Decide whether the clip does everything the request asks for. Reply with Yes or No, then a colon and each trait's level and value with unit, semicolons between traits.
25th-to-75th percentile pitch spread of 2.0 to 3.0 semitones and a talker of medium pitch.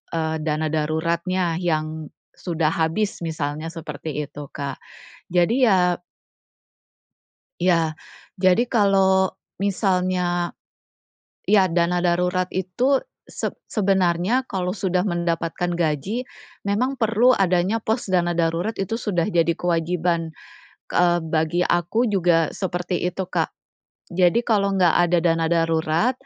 Yes: average, 2.7 semitones; medium, 175 Hz